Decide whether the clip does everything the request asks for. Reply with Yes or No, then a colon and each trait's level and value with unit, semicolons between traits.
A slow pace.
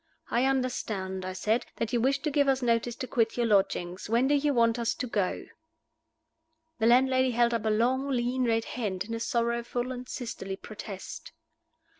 No: average, 185 wpm